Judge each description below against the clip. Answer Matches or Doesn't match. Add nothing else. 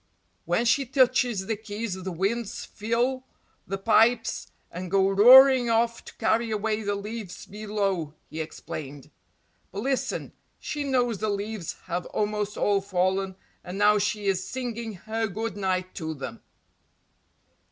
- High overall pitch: Matches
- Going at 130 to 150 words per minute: Matches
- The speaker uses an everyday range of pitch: Matches